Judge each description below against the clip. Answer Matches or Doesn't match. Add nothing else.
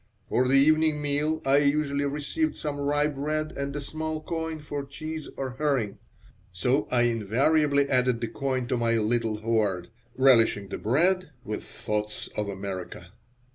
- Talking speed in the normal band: Matches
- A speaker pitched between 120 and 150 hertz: Matches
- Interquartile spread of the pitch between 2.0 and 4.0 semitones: Doesn't match